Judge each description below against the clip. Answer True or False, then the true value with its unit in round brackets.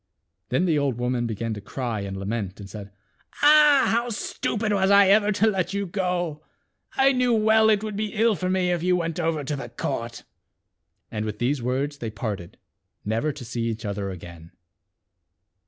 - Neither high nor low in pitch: True (150 Hz)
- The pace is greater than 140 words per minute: True (190 wpm)